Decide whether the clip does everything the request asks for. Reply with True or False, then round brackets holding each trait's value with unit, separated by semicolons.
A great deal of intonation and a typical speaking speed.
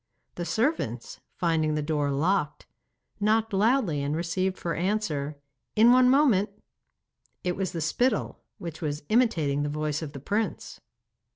True (6.1 semitones; 145 wpm)